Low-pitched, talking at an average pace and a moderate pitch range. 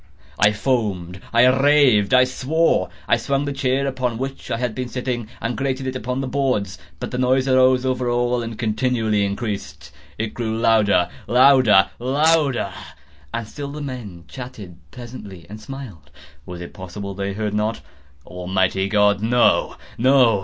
Yes: low, 120 Hz; average, 145 wpm; average, 4.2 semitones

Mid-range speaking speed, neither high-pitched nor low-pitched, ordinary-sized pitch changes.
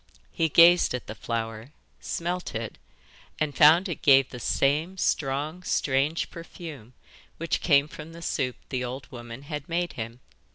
Yes: average, 155 wpm; medium, 145 Hz; average, 4.9 semitones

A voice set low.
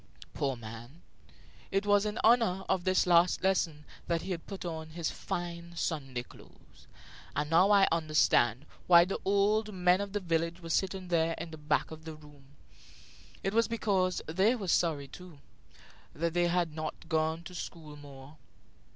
No: medium, 170 Hz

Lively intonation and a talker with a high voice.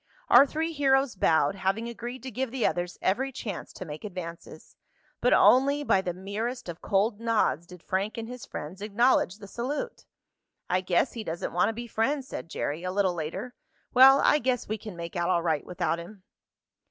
Yes: wide, 5.8 semitones; high, 210 Hz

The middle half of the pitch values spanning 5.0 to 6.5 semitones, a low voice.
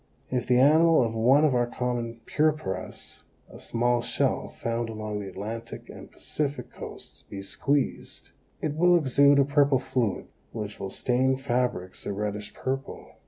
No: average, 4.1 semitones; low, 125 Hz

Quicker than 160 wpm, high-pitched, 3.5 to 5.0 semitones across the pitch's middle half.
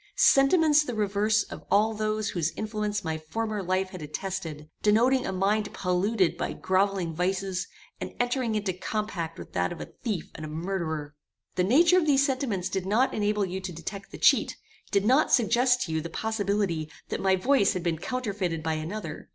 Yes: average, 185 wpm; high, 200 Hz; average, 3.8 semitones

